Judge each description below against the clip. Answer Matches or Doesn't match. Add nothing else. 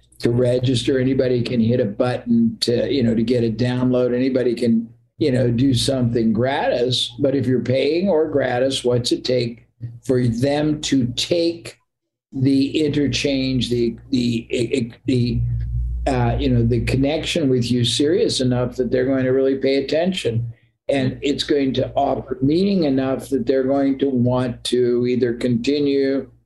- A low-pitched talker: Matches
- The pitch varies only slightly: Matches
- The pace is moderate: Matches